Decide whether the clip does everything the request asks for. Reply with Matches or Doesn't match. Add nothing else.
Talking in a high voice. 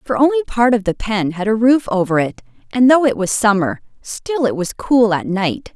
Matches